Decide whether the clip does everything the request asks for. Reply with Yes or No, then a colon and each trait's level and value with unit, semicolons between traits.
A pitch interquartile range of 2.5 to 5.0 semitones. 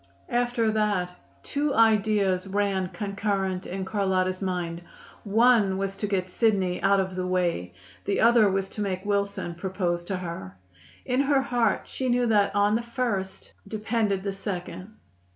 Yes: average, 2.9 semitones